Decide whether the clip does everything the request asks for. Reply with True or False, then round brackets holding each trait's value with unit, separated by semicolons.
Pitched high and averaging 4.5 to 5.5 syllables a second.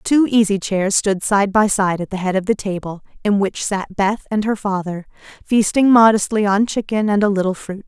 True (200 Hz; 5.0 syllables/s)